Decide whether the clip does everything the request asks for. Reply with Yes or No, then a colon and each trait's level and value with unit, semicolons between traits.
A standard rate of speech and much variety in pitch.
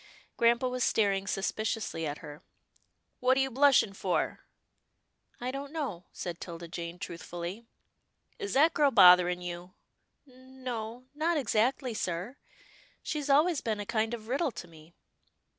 Yes: average, 160 wpm; wide, 6.8 semitones